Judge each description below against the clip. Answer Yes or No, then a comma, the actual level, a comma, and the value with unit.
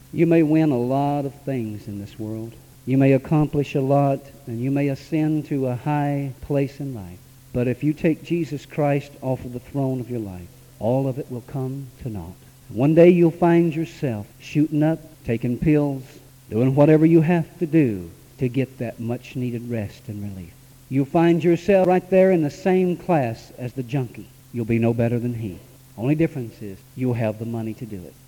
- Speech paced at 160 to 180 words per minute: No, average, 200 wpm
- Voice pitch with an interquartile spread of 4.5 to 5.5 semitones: No, average, 3.8 semitones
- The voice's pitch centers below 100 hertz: No, low, 135 Hz